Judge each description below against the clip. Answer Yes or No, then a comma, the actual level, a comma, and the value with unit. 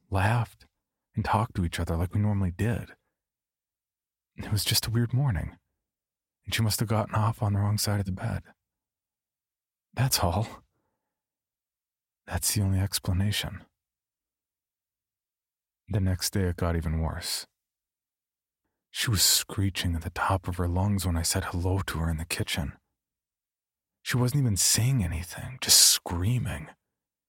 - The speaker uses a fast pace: No, average, 145 wpm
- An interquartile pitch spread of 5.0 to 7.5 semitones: No, average, 3.6 semitones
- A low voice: Yes, very low, 95 Hz